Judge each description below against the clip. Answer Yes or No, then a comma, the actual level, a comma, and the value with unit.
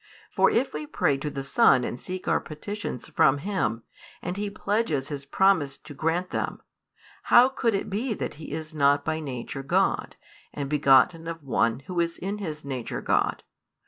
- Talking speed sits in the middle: Yes, average, 180 wpm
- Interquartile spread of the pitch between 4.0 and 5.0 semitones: No, wide, 5.6 semitones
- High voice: No, medium, 155 Hz